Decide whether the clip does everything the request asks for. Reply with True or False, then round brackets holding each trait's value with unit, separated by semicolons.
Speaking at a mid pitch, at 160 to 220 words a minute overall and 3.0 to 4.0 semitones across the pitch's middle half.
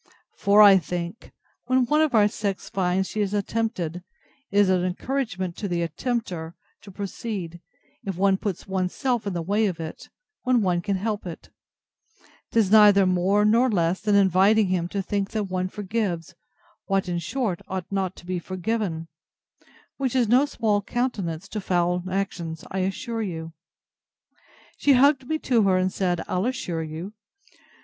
False (195 Hz; 170 wpm; 3.5 semitones)